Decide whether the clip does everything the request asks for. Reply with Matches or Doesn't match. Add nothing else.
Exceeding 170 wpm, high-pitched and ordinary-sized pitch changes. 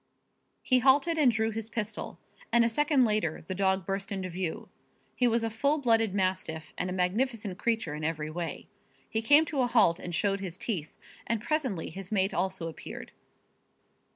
Matches